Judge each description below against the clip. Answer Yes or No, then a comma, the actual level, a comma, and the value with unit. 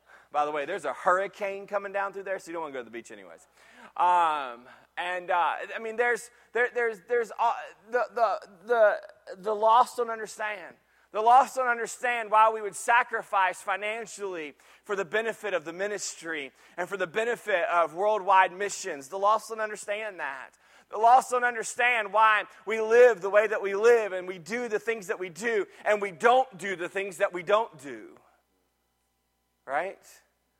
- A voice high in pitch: Yes, high, 210 Hz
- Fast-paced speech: No, average, 185 wpm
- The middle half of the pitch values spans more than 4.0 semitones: No, average, 3.3 semitones